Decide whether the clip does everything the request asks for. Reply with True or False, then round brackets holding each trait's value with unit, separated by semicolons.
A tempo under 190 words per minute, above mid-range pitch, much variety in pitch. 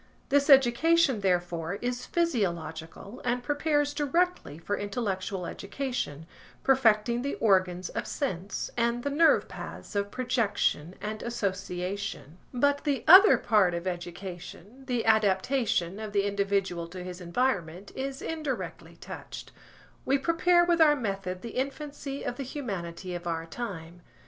True (135 wpm; 215 Hz; 6.9 semitones)